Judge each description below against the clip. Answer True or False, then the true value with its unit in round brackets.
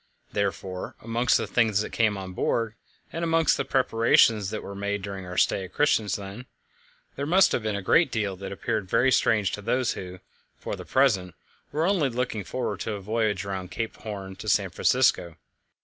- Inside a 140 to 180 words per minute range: False (190 wpm)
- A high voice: False (105 Hz)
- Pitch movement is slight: False (4.1 semitones)